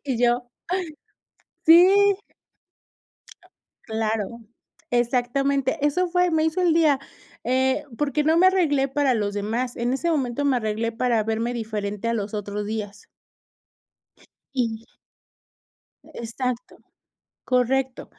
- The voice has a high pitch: Yes, high, 245 Hz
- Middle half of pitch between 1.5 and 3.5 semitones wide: No, average, 4.3 semitones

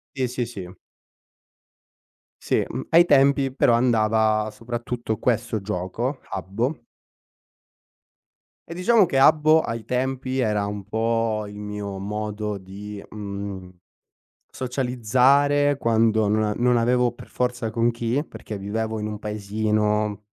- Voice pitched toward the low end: Yes, low, 115 Hz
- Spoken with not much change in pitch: No, average, 3.1 semitones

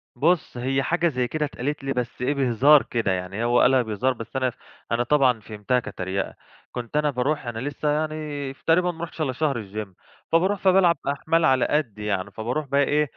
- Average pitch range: Yes, average, 4.1 semitones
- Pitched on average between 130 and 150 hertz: Yes, low, 135 Hz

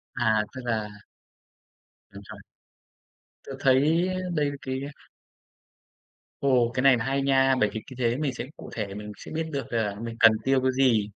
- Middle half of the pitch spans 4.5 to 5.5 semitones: No, average, 3.3 semitones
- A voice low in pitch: Yes, low, 130 Hz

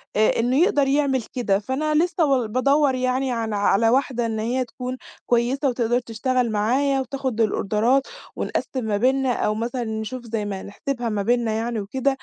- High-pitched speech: Yes, high, 245 Hz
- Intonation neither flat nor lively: Yes, average, 3.2 semitones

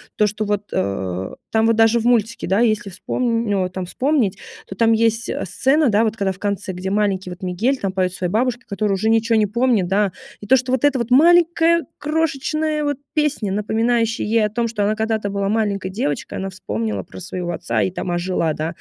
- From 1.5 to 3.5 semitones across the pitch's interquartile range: No, average, 4.1 semitones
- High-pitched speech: Yes, high, 215 Hz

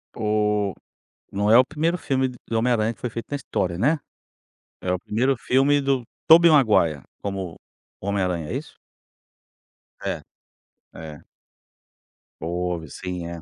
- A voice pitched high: No, low, 105 Hz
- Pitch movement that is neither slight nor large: No, wide, 6.5 semitones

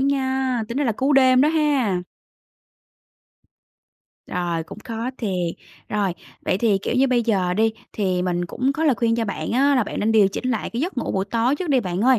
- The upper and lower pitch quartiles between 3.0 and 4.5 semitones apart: No, average, 5.1 semitones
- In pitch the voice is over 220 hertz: Yes, high, 230 Hz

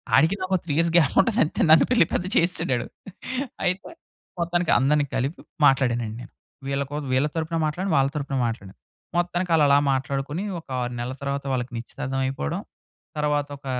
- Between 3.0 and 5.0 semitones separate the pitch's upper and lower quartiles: Yes, average, 4.1 semitones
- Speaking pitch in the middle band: Yes, medium, 145 Hz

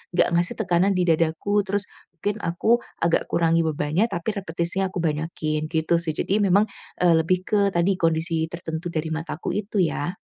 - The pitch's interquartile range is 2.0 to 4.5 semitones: Yes, average, 3.2 semitones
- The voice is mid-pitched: Yes, medium, 170 Hz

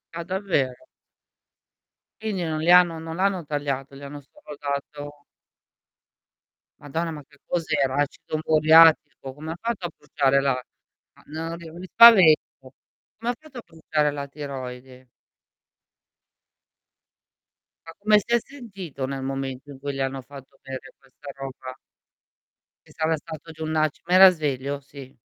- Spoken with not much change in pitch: No, average, 3.6 semitones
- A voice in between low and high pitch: Yes, medium, 150 Hz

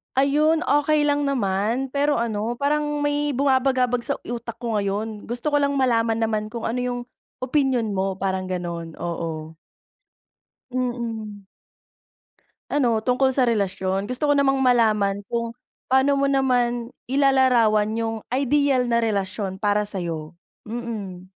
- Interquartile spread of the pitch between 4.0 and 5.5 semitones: Yes, average, 4.5 semitones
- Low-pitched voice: No, high, 235 Hz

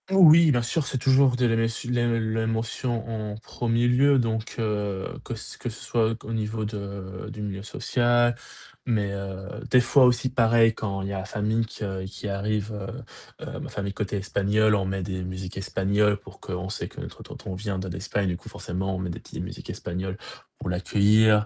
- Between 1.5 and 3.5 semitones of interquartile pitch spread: Yes, average, 3.2 semitones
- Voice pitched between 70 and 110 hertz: Yes, low, 105 Hz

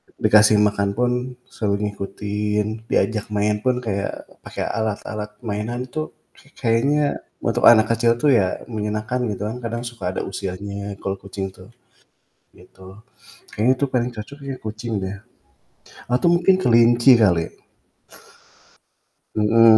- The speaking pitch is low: Yes, low, 110 Hz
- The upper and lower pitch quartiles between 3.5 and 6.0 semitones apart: No, average, 2.7 semitones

